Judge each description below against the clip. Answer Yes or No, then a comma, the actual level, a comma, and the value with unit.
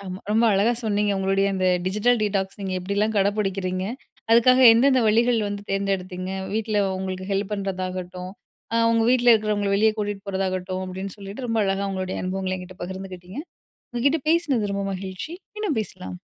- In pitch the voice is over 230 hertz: No, high, 195 Hz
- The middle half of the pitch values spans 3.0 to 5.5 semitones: No, narrow, 2.6 semitones